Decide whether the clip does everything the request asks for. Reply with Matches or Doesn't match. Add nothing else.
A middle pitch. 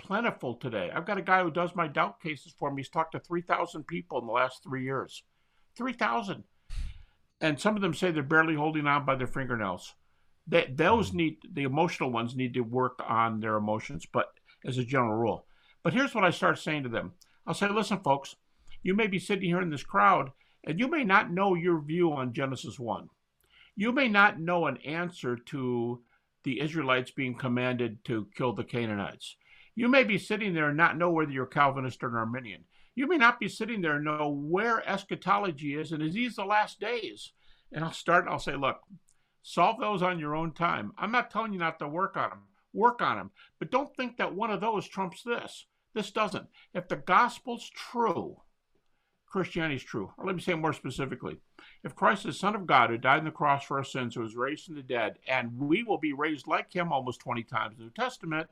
Matches